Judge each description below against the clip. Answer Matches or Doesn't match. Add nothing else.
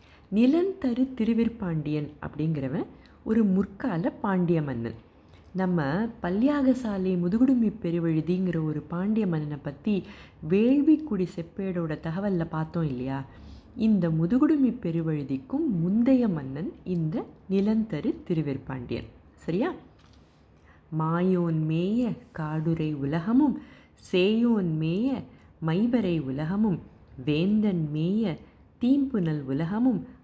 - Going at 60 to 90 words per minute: Matches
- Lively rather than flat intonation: Matches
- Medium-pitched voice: Matches